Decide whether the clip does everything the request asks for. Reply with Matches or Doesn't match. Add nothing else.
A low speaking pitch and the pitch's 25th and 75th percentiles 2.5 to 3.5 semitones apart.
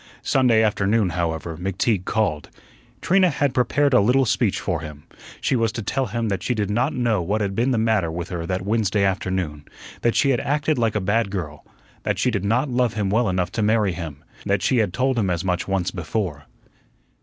Doesn't match